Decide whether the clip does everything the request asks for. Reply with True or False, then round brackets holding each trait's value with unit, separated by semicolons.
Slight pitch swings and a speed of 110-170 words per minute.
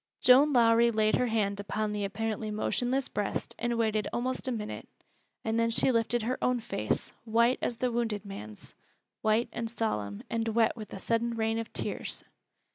False (1.9 semitones; 180 wpm)